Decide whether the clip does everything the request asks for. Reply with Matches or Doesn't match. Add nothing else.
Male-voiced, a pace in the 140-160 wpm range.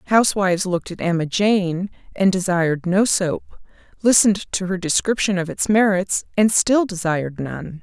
Doesn't match